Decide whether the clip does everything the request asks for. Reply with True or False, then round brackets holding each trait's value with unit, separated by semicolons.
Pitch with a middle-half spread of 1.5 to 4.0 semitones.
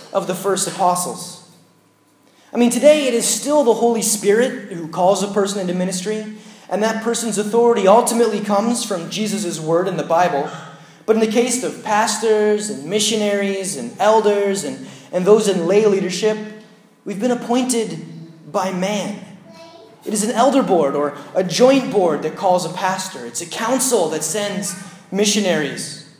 True (3.4 semitones)